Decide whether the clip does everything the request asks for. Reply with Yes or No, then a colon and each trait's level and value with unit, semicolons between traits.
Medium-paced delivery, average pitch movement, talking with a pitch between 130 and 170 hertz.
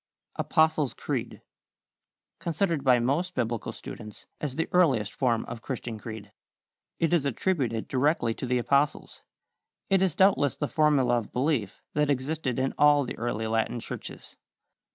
Yes: average, 145 wpm; average, 4.7 semitones; low, 135 Hz